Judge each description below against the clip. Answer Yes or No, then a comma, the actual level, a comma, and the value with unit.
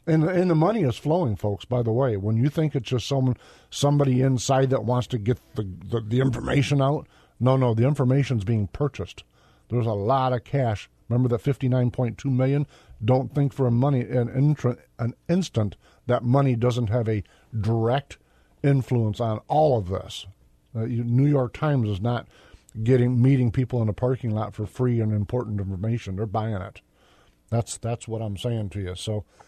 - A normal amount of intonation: Yes, average, 3.4 semitones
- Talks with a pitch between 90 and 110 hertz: No, low, 120 Hz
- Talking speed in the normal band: Yes, average, 190 wpm